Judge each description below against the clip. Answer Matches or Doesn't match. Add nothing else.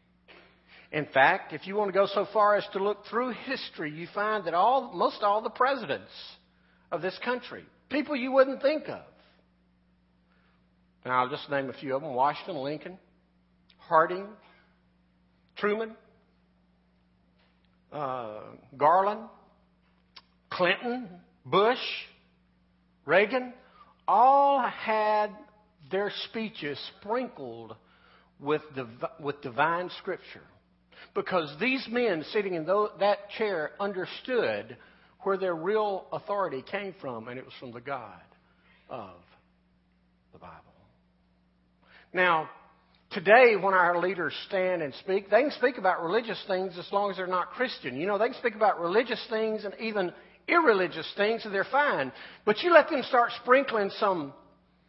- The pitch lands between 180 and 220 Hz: Matches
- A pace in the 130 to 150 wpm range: Matches